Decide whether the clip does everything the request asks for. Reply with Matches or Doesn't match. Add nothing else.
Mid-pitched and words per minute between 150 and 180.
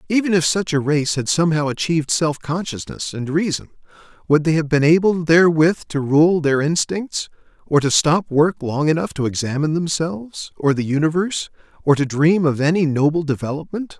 Matches